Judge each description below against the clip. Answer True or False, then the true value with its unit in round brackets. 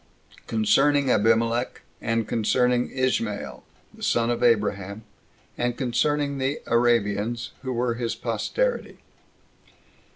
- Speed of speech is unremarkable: False (100 wpm)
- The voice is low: True (120 Hz)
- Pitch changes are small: True (2.3 semitones)